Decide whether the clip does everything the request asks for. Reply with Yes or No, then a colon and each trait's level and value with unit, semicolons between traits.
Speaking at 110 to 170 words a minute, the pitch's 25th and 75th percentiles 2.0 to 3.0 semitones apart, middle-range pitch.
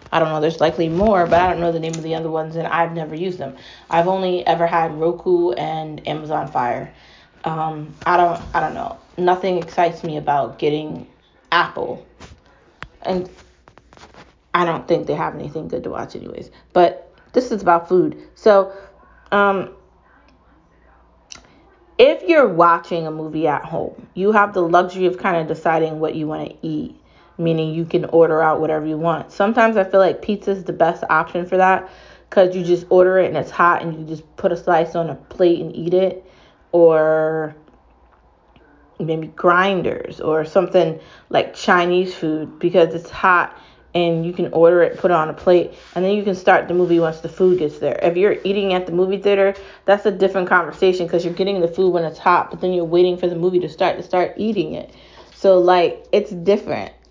No: average, 195 wpm; narrow, 2.4 semitones; medium, 175 Hz